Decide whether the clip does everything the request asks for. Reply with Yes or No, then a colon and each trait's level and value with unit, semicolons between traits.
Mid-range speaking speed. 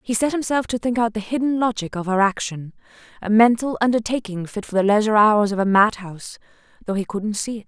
No: fast, 210 wpm